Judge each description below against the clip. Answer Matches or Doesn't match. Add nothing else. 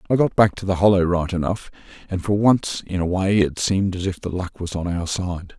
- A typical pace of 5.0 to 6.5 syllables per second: Matches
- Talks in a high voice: Doesn't match